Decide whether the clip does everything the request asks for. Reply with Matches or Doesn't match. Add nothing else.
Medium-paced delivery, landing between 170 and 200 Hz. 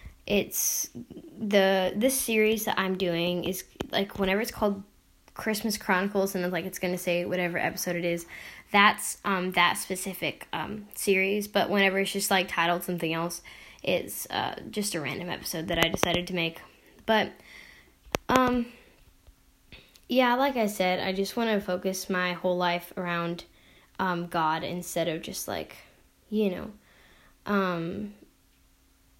Matches